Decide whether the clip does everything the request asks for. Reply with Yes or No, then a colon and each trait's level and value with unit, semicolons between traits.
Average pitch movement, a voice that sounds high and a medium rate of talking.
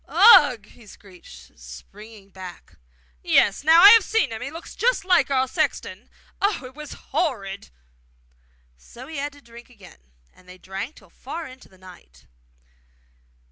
No: wide, 7.8 semitones; high, 235 Hz; average, 160 wpm